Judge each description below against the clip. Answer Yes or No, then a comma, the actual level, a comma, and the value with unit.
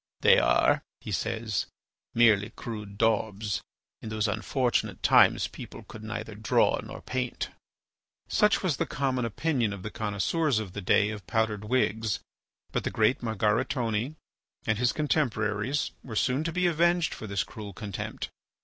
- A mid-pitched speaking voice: No, low, 110 Hz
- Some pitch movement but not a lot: Yes, average, 3.6 semitones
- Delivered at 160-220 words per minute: No, average, 150 wpm